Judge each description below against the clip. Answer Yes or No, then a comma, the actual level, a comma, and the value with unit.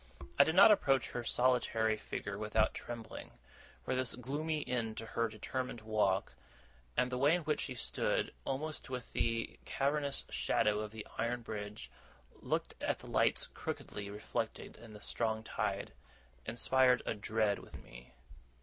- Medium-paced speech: Yes, average, 155 wpm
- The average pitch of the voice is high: No, low, 115 Hz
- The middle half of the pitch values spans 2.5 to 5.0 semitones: Yes, average, 3.3 semitones